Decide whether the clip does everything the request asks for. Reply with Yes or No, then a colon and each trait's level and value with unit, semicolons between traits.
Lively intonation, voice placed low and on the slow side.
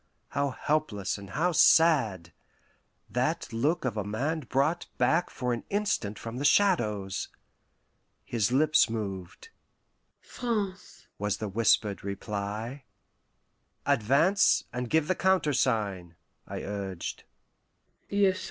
Yes: wide, 7.3 semitones; low, 120 Hz; slow, 105 wpm